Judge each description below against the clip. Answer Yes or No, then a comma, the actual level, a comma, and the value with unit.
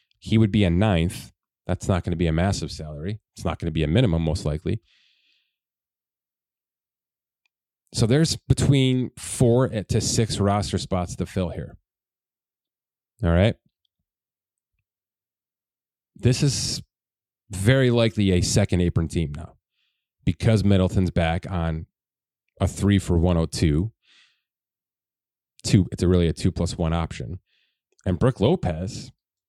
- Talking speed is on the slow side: Yes, slow, 130 wpm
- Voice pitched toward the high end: No, very low, 95 Hz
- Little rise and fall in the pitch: No, average, 4.5 semitones